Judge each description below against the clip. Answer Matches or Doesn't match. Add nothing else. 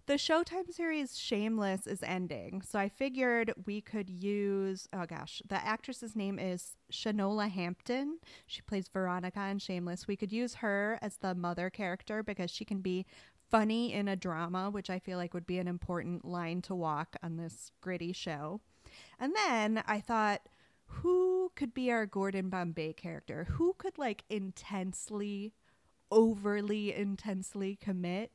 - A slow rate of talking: Doesn't match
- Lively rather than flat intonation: Doesn't match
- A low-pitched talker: Doesn't match